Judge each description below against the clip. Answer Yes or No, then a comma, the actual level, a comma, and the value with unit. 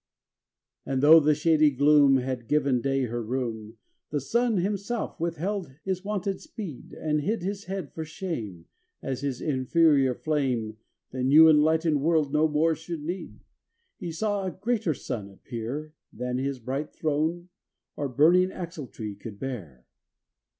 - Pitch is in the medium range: Yes, medium, 150 Hz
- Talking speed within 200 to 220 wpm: No, average, 150 wpm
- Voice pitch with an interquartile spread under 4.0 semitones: No, average, 4.7 semitones